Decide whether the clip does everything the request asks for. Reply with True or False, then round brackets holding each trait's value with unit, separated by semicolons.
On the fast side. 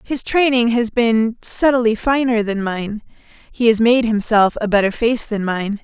False (175 wpm)